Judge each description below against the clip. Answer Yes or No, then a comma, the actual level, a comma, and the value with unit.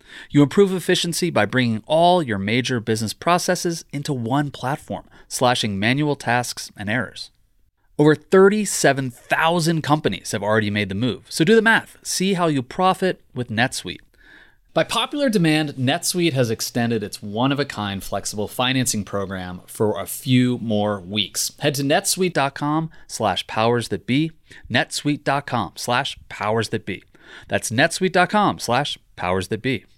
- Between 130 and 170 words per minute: Yes, average, 140 wpm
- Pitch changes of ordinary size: No, wide, 7.1 semitones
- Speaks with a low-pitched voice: Yes, low, 130 Hz